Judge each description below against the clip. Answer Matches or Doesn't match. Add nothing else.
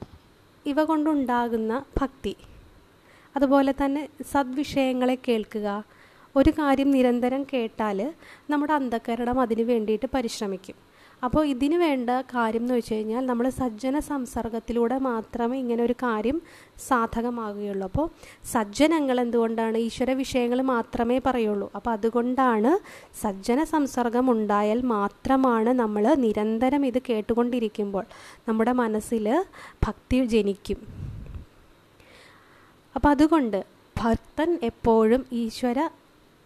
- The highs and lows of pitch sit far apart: Doesn't match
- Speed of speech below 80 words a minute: Doesn't match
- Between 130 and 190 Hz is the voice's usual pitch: Doesn't match